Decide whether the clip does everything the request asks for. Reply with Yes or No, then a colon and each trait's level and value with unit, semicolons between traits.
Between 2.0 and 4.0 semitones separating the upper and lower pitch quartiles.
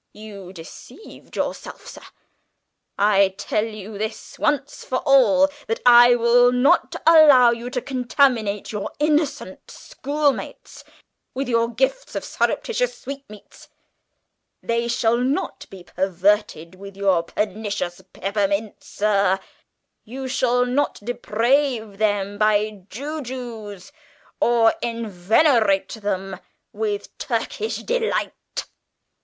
No: average, 4.7 semitones